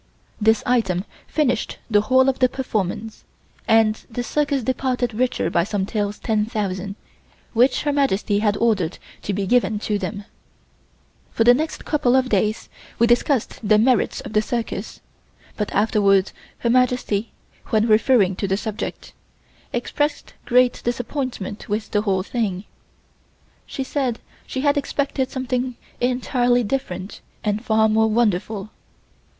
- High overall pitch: Yes, high, 225 Hz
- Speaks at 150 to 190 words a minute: No, average, 140 wpm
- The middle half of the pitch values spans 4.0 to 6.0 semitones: No, average, 3.5 semitones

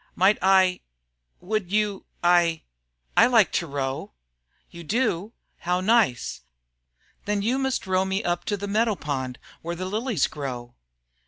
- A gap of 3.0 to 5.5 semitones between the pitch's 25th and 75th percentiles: Yes, average, 4.1 semitones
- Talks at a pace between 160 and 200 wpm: No, average, 145 wpm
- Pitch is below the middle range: No, medium, 185 Hz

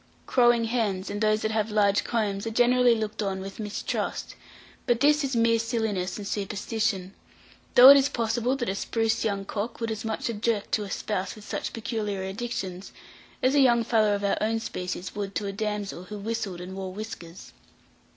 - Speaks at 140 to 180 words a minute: No, average, 195 wpm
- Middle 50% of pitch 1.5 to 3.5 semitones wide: Yes, narrow, 2.6 semitones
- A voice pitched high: Yes, high, 215 Hz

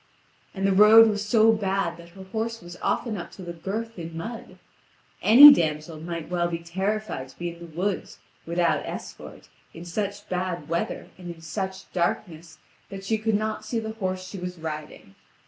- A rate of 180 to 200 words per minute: Yes, average, 185 wpm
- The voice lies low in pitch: No, medium, 185 Hz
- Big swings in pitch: No, average, 3.9 semitones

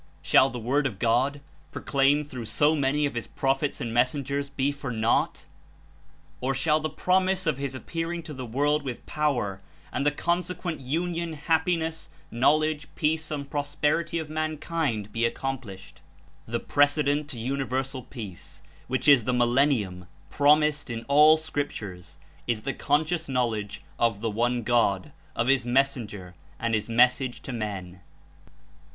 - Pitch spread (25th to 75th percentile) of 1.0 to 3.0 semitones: No, average, 4.3 semitones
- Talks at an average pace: Yes, average, 155 wpm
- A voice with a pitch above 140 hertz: No, low, 135 Hz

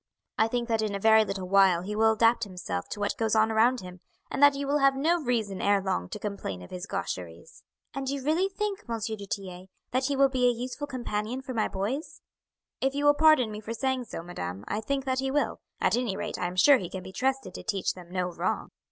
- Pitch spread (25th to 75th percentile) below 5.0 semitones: No, wide, 5.6 semitones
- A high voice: Yes, high, 225 Hz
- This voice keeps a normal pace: No, fast, 245 wpm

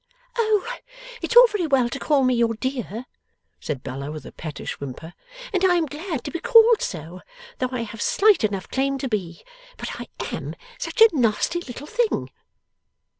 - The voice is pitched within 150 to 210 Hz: No, very high, 260 Hz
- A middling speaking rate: Yes, average, 180 wpm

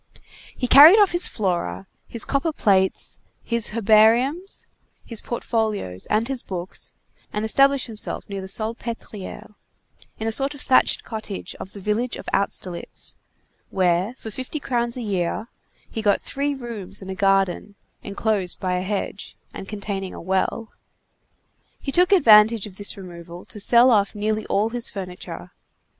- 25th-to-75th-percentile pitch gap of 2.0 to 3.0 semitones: No, average, 3.7 semitones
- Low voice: No, high, 215 Hz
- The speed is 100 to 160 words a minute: Yes, average, 150 wpm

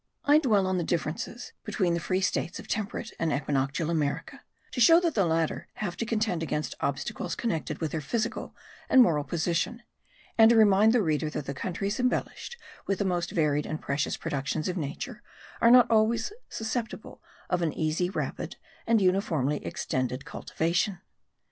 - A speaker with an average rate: Yes, average, 170 wpm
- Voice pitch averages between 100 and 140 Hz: No, medium, 180 Hz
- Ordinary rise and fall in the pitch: No, wide, 6.2 semitones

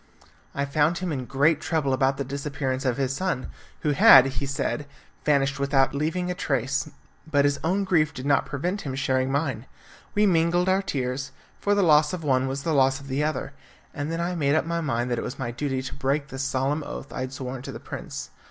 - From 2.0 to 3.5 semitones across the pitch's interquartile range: Yes, average, 2.9 semitones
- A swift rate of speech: Yes, fast, 225 wpm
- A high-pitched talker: No, medium, 140 Hz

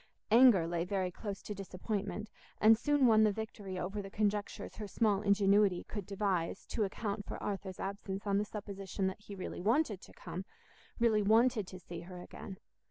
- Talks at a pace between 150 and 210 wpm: Yes, average, 180 wpm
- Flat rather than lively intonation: Yes, narrow, 2.1 semitones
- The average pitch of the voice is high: Yes, high, 200 Hz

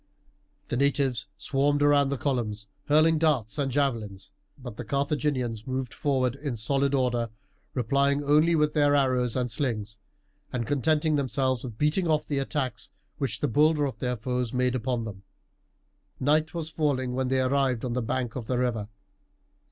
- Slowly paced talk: No, average, 165 wpm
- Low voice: Yes, low, 130 Hz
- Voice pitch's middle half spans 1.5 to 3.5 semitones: Yes, average, 3.0 semitones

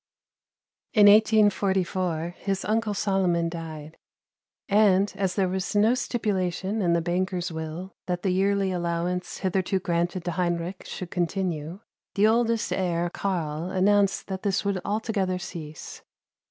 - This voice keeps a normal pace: No, slow, 130 wpm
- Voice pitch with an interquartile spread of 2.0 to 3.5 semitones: Yes, narrow, 2.6 semitones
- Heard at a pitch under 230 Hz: Yes, medium, 185 Hz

